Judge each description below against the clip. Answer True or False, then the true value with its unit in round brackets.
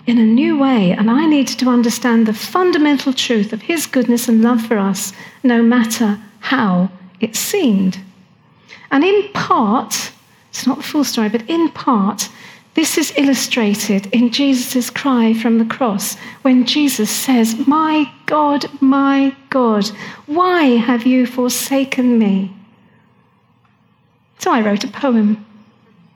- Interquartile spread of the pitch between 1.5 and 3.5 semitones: False (4.2 semitones)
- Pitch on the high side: True (240 Hz)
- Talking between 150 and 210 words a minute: False (140 wpm)